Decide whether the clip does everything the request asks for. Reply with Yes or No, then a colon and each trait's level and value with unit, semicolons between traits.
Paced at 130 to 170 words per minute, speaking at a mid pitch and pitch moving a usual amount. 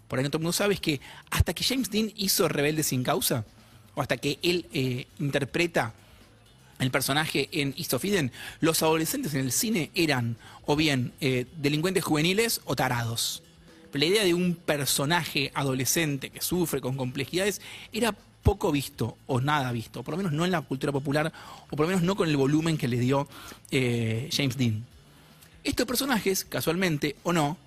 No: average, 180 wpm; medium, 145 Hz; average, 4.8 semitones